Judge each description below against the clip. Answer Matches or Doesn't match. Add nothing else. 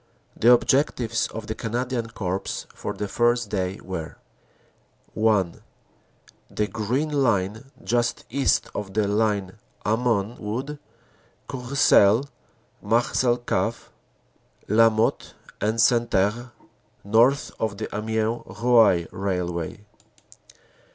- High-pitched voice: Doesn't match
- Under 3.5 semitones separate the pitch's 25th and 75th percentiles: Matches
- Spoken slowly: Matches